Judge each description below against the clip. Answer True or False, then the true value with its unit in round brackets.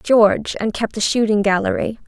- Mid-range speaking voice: False (215 Hz)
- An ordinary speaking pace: True (175 wpm)